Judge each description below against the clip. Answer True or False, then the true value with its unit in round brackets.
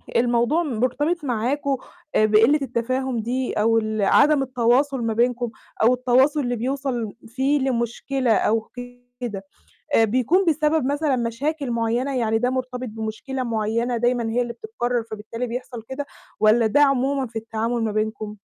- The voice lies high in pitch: True (245 Hz)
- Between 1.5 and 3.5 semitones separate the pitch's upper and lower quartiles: True (3.0 semitones)